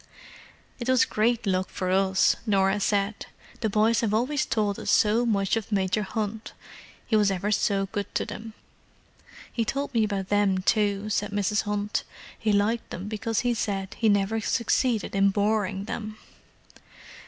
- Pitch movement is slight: Yes, narrow, 2.1 semitones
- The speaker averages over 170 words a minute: No, average, 165 wpm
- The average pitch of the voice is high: Yes, high, 210 Hz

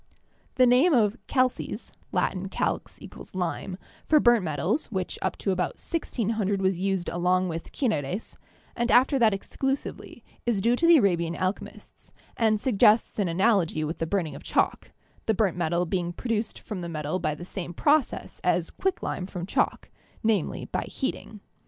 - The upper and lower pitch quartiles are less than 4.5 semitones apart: No, average, 5.1 semitones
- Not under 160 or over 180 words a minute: Yes, average, 165 wpm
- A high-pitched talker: Yes, high, 195 Hz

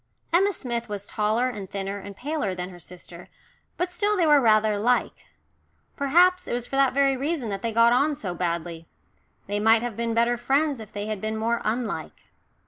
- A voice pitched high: Yes, high, 230 Hz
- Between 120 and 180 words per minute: No, average, 200 wpm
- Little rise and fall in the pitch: No, average, 5.1 semitones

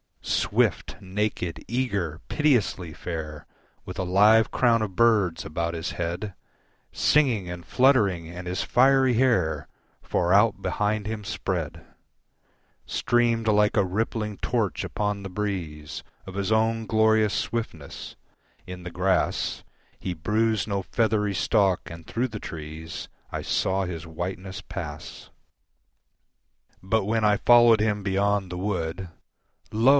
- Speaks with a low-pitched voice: Yes, low, 100 Hz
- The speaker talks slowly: Yes, slow, 130 wpm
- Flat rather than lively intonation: No, average, 3.8 semitones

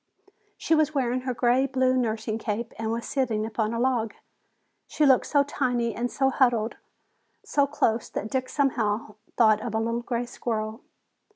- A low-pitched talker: No, high, 240 Hz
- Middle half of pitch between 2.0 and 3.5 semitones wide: Yes, average, 2.8 semitones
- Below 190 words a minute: Yes, average, 170 wpm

